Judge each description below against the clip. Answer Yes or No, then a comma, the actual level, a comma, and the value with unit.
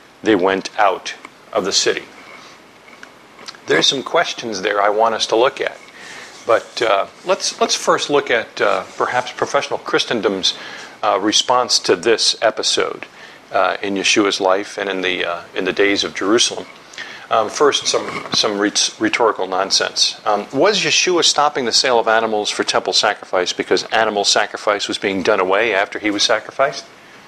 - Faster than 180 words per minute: No, average, 165 wpm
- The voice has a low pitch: Yes, low, 100 Hz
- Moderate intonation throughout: No, narrow, 1.8 semitones